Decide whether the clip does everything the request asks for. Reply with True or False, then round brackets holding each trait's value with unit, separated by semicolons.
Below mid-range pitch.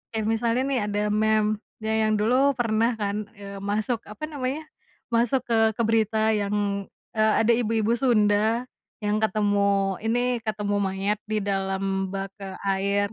False (215 Hz)